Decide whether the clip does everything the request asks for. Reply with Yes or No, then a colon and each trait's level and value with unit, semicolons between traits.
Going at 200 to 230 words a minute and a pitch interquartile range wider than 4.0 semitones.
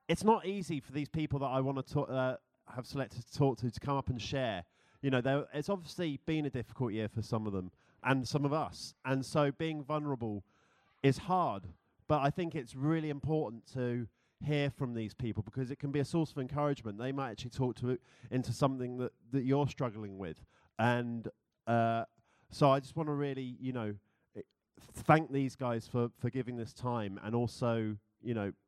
No: fast, 205 wpm; average, 3.6 semitones